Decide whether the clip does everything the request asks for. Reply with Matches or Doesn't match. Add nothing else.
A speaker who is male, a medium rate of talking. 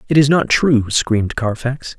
Matches